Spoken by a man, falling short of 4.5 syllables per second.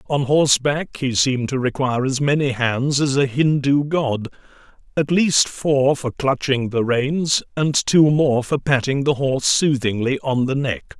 Yes: male; 4.3 syllables/s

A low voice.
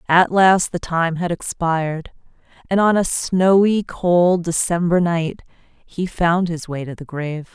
No: medium, 175 Hz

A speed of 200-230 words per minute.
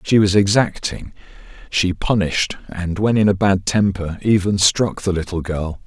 No: average, 165 wpm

